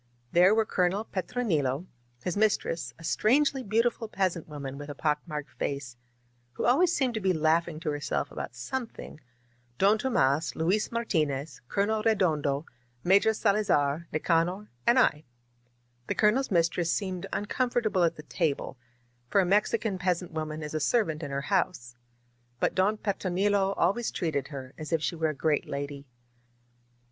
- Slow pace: No, average, 160 wpm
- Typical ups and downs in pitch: No, wide, 5.7 semitones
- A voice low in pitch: No, medium, 175 Hz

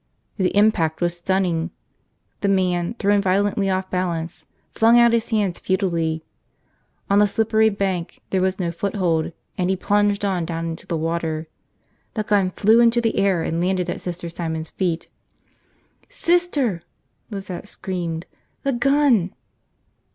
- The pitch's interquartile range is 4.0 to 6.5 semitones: No, average, 3.3 semitones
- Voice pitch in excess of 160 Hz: Yes, high, 190 Hz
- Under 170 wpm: Yes, average, 145 wpm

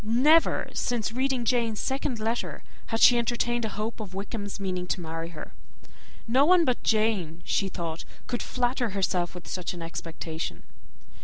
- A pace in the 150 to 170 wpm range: Yes, average, 160 wpm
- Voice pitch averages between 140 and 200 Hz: No, high, 220 Hz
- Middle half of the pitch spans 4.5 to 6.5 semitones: Yes, average, 5.1 semitones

